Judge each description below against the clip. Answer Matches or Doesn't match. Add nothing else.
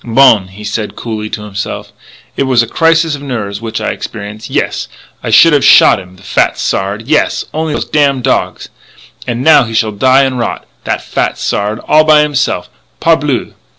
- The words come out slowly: Doesn't match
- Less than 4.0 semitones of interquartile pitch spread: Doesn't match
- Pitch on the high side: Doesn't match